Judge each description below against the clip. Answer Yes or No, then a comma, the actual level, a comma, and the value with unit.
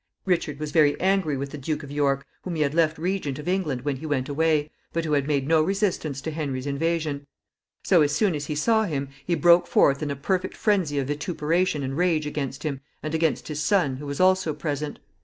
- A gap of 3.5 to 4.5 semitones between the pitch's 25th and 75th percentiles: No, average, 3.1 semitones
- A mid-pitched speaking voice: Yes, medium, 150 Hz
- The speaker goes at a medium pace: No, fast, 225 wpm